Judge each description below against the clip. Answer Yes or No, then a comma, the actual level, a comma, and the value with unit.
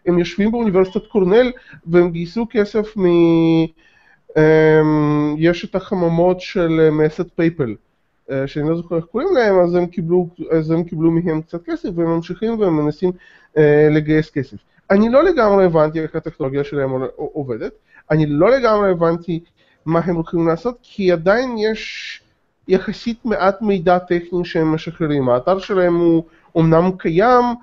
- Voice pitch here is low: No, medium, 175 Hz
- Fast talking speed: No, average, 140 wpm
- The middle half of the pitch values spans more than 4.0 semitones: No, average, 3.4 semitones